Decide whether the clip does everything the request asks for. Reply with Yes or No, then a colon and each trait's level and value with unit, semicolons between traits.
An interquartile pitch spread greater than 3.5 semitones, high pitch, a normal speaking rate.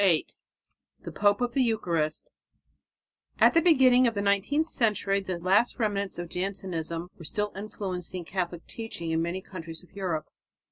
Yes: average, 4.0 semitones; high, 195 Hz; average, 155 wpm